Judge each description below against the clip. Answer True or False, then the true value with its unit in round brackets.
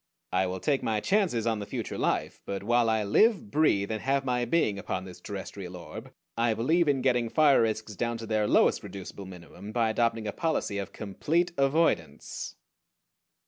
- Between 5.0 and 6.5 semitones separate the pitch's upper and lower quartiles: True (5.3 semitones)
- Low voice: True (115 Hz)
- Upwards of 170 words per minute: True (185 wpm)